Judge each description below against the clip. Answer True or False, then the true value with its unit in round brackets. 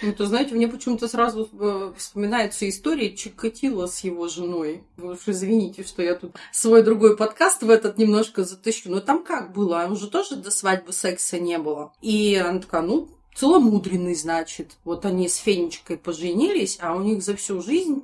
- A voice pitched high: True (205 Hz)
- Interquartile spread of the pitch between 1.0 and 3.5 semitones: False (4.0 semitones)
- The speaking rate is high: True (175 wpm)